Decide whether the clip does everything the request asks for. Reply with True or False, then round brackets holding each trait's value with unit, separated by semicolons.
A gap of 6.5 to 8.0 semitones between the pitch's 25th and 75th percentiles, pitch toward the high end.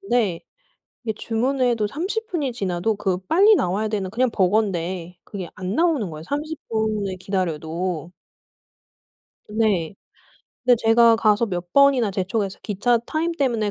False (5.2 semitones; 215 Hz)